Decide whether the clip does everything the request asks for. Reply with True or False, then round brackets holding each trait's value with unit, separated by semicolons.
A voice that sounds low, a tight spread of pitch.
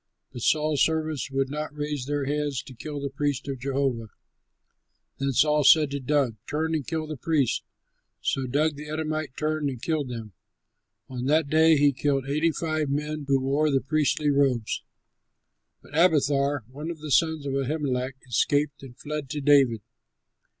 False (145 Hz; 2.1 semitones)